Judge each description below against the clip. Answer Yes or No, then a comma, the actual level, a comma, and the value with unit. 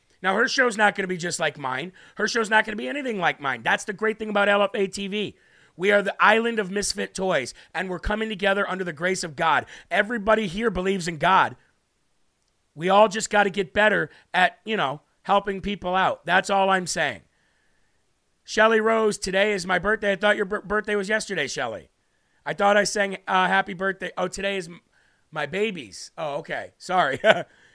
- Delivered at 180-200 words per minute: Yes, average, 195 wpm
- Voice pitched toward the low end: No, high, 200 Hz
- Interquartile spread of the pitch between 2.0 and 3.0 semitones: Yes, narrow, 2.4 semitones